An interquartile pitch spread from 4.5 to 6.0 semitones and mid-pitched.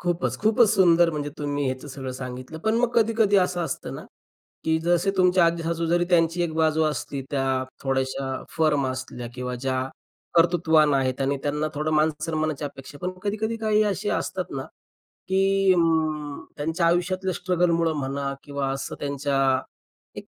No: average, 4.1 semitones; medium, 160 Hz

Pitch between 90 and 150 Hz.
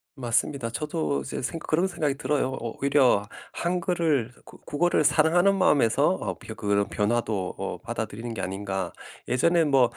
Yes: low, 135 Hz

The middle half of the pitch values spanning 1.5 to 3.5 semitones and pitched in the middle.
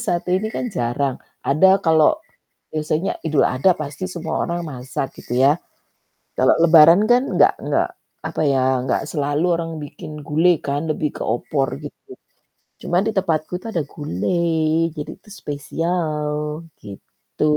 Yes: average, 2.9 semitones; medium, 155 Hz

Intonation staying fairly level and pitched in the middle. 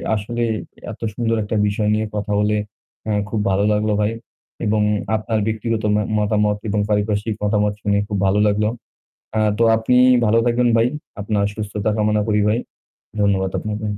No: narrow, 1.1 semitones; low, 105 Hz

